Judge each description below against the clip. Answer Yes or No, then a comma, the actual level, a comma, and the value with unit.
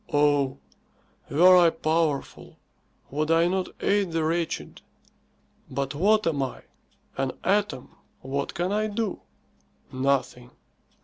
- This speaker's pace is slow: Yes, slow, 115 wpm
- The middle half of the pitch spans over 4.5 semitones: Yes, average, 4.9 semitones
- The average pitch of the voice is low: No, medium, 160 Hz